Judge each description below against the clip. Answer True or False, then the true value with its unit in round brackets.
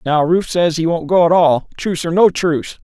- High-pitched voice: False (165 Hz)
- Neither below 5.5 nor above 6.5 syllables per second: True (5.7 syllables/s)